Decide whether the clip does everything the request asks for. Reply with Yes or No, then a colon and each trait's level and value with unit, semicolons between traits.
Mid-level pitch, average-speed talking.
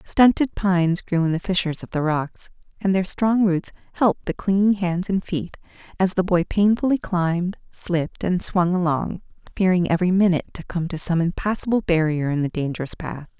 Yes: medium, 180 Hz; average, 185 wpm